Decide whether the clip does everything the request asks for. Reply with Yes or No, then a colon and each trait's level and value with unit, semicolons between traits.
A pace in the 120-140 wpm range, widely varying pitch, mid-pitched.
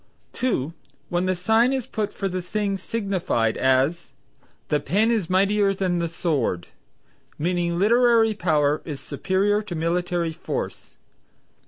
No: slow, 135 wpm; average, 4.1 semitones; medium, 180 Hz